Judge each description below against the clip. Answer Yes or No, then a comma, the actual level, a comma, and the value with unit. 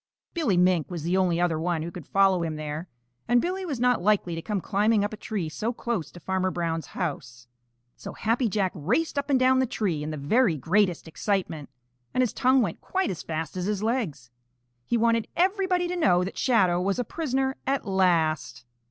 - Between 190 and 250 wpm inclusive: Yes, fast, 205 wpm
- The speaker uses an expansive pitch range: Yes, wide, 6.4 semitones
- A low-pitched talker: No, high, 190 Hz